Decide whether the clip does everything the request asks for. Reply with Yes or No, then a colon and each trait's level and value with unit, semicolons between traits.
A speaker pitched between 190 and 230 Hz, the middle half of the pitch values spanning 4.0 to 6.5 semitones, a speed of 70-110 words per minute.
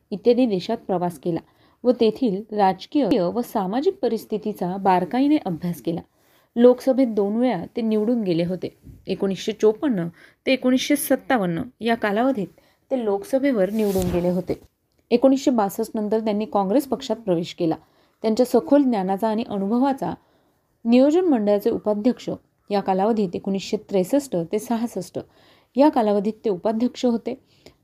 No: high, 220 Hz; average, 4.4 semitones; average, 125 wpm